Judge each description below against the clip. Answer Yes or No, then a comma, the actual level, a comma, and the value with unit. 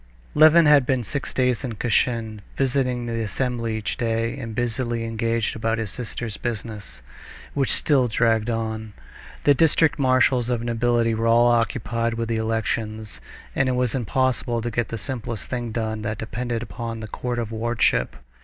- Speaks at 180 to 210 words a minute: No, average, 165 wpm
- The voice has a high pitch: No, low, 115 Hz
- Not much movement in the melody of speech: Yes, narrow, 1.9 semitones